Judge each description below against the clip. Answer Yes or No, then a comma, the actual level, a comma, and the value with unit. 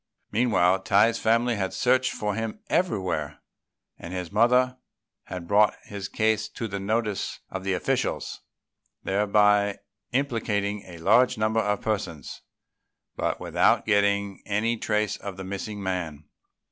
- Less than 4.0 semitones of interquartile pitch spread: Yes, average, 2.7 semitones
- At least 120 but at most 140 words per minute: Yes, slow, 135 wpm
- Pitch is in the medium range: No, low, 105 Hz